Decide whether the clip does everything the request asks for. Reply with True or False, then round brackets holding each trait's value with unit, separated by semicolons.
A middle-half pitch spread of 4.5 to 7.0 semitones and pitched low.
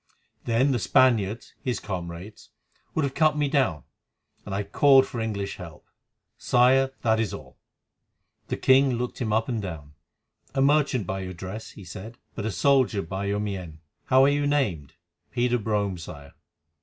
True (5.6 semitones; 110 Hz)